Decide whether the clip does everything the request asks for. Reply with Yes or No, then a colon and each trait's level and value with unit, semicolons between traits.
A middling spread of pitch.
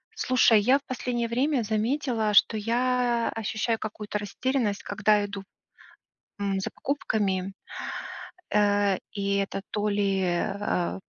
Yes: average, 3.0 semitones